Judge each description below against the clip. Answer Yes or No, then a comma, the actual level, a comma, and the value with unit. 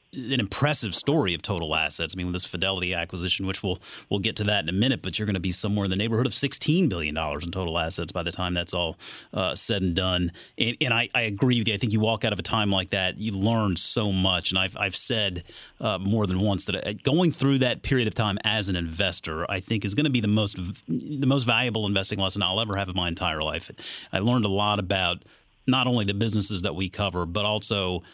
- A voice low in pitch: Yes, low, 100 Hz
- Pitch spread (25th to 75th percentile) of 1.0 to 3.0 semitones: No, average, 3.6 semitones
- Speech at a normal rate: No, fast, 255 wpm